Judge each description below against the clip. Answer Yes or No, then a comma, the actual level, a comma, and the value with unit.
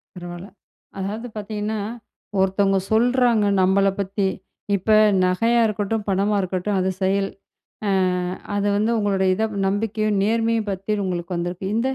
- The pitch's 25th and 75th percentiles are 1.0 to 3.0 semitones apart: Yes, narrow, 2.4 semitones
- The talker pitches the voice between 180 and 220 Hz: Yes, high, 200 Hz